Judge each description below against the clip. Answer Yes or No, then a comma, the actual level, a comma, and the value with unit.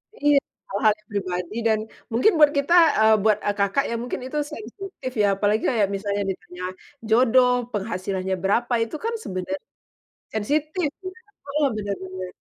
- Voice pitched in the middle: No, high, 220 Hz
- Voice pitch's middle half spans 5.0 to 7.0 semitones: Yes, wide, 5.5 semitones